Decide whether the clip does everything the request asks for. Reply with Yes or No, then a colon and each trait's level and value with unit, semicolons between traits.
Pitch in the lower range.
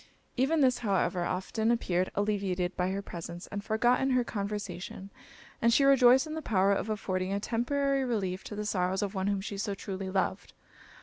No: high, 200 Hz